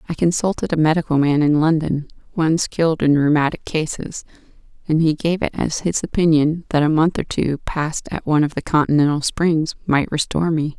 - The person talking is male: No, female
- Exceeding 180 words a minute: Yes, average, 190 wpm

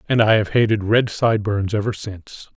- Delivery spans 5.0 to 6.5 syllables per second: Yes, 5.5 syllables/s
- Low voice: Yes, low, 105 Hz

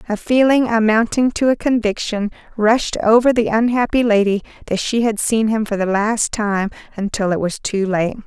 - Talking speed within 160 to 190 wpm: Yes, average, 180 wpm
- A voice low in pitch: No, high, 220 Hz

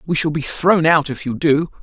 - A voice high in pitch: No, medium, 155 Hz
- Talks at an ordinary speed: No, fast, 265 wpm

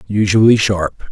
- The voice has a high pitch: No, low, 100 Hz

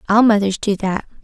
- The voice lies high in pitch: Yes, high, 210 Hz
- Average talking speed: Yes, average, 195 wpm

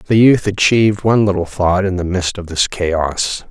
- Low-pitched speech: Yes, very low, 95 Hz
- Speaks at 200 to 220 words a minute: Yes, fast, 205 wpm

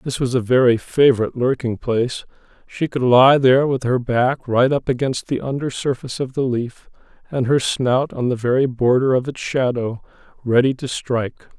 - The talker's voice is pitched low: Yes, low, 125 Hz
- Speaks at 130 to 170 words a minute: No, average, 185 wpm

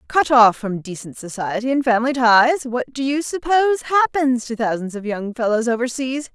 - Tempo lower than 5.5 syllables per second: Yes, 5.3 syllables/s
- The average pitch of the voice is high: Yes, very high, 250 Hz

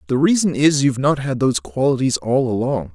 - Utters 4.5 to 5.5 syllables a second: No, 5.8 syllables/s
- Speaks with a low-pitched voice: Yes, low, 130 Hz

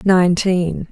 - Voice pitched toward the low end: No, medium, 180 Hz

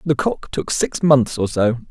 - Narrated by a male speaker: Yes, male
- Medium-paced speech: Yes, average, 190 wpm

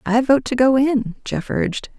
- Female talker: Yes, female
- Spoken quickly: Yes, fast, 210 wpm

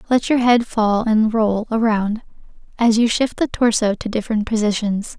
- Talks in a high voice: Yes, high, 220 Hz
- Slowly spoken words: No, average, 175 wpm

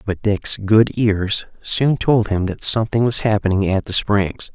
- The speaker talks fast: No, average, 185 wpm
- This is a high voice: No, low, 105 Hz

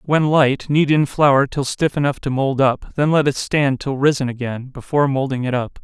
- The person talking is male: Yes, male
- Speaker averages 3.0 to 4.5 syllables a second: No, 4.9 syllables/s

